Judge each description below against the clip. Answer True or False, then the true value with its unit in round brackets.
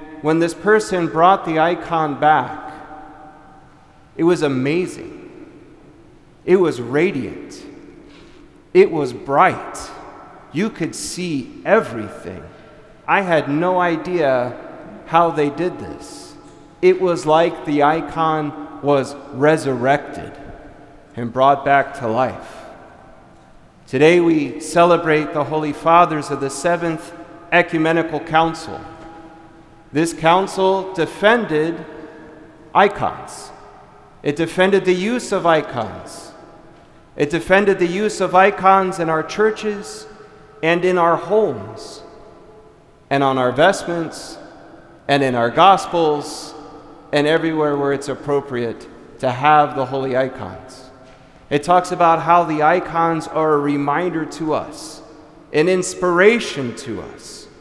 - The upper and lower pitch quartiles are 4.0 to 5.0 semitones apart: False (3.0 semitones)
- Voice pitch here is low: False (160 Hz)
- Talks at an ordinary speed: False (110 wpm)